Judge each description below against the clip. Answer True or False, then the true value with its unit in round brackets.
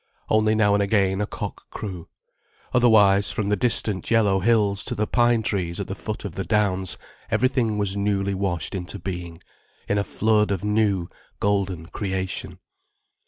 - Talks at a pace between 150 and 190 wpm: True (165 wpm)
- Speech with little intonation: True (2.1 semitones)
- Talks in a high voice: False (100 Hz)